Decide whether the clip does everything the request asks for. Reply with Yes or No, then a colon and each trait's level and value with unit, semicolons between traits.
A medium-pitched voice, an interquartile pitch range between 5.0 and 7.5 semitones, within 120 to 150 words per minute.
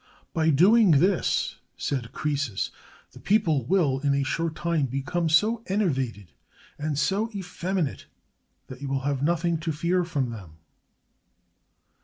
No: medium, 155 Hz; average, 4.6 semitones; slow, 135 wpm